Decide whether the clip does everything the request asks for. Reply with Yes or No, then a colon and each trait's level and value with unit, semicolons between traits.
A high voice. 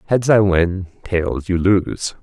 No: very low, 95 Hz